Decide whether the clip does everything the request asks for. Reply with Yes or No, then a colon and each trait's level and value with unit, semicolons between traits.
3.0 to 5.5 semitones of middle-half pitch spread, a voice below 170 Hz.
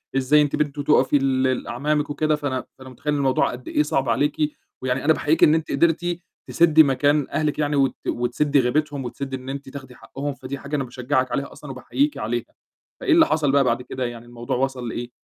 No: narrow, 2.5 semitones; medium, 140 Hz